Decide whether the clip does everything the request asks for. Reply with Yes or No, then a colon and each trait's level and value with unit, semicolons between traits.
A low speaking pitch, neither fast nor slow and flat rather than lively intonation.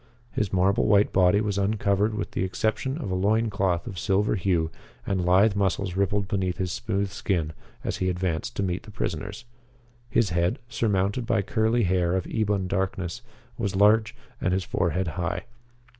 Yes: very low, 95 Hz; average, 175 wpm; narrow, 2.3 semitones